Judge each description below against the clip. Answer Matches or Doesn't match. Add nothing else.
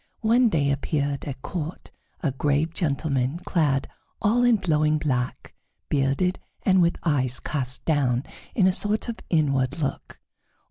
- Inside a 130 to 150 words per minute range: Matches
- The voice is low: Doesn't match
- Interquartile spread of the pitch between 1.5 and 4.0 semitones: Doesn't match